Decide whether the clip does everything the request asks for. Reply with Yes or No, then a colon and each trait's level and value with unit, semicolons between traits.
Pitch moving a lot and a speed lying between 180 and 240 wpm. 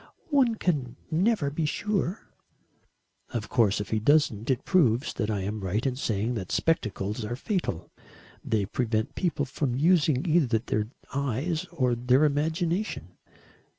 No: wide, 6.8 semitones; average, 145 wpm